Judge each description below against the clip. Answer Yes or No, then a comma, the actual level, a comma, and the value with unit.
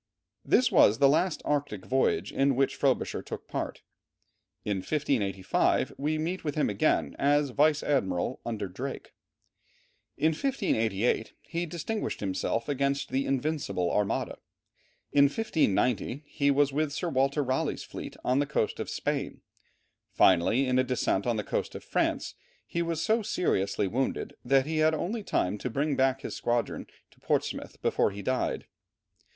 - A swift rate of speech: No, average, 155 wpm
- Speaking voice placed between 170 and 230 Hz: No, low, 135 Hz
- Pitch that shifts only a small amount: No, average, 5.1 semitones